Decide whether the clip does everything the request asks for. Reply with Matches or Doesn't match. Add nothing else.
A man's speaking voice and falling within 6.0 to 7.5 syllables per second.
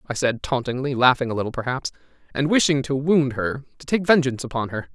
Matches